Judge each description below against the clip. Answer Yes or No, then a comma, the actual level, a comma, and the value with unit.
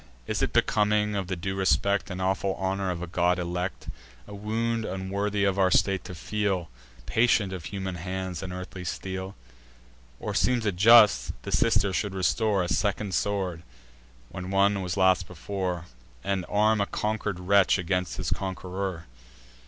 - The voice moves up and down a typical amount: No, narrow, 1.9 semitones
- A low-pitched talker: Yes, very low, 95 Hz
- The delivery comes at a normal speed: Yes, average, 160 wpm